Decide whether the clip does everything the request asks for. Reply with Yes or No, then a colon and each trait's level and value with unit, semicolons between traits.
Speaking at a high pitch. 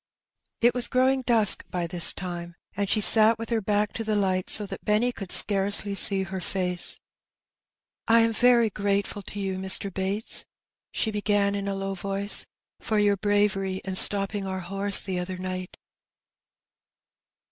Yes: high, 200 Hz